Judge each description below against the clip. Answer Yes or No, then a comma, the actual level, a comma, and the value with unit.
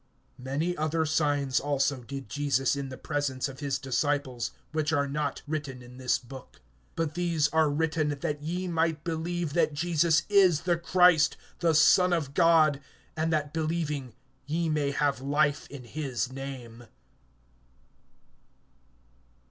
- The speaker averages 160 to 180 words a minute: No, average, 140 wpm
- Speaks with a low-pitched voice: No, medium, 150 Hz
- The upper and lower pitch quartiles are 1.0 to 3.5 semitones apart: Yes, average, 2.8 semitones